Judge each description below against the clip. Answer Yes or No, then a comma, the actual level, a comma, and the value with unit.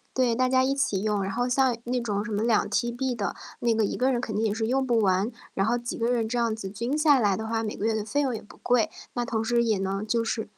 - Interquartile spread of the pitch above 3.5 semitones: No, narrow, 2.6 semitones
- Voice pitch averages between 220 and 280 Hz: Yes, high, 230 Hz